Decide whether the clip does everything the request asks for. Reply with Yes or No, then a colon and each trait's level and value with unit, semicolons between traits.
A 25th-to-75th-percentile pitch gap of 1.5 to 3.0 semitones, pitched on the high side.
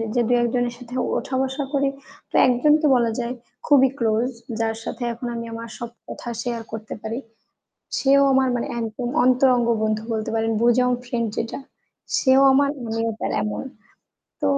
Yes: narrow, 2.4 semitones; high, 240 Hz